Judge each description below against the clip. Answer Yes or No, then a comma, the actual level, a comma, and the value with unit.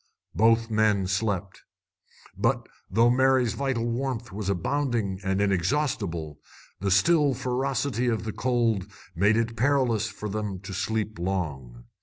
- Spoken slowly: Yes, slow, 130 wpm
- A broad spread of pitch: No, average, 4.2 semitones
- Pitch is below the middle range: Yes, low, 110 Hz